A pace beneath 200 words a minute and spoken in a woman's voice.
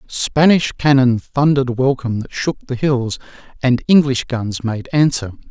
No: average, 155 wpm; male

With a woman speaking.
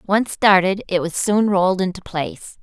Yes: female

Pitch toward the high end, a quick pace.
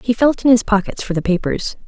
Yes: high, 215 Hz; fast, 255 wpm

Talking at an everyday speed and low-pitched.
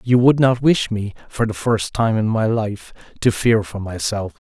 No: fast, 215 wpm; low, 110 Hz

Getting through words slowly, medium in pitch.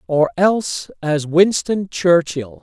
Yes: slow, 115 wpm; medium, 165 Hz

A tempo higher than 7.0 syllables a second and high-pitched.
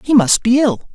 No: 4.9 syllables/s; high, 245 Hz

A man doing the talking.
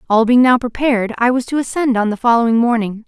No: female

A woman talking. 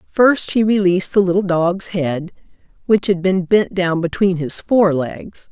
Yes: female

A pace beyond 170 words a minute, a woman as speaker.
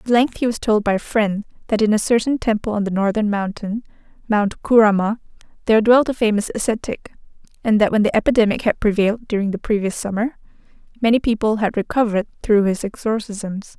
Yes: average, 185 wpm; female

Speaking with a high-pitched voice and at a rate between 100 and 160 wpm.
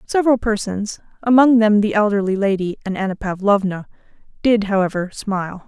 Yes: high, 205 Hz; slow, 135 wpm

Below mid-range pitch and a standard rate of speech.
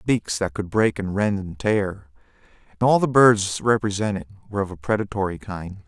Yes: low, 100 Hz; average, 165 wpm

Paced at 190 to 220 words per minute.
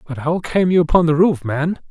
No: fast, 250 wpm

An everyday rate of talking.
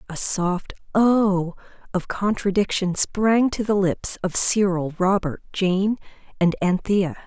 No: slow, 125 wpm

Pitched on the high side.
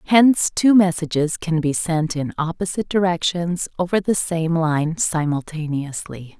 No: medium, 170 Hz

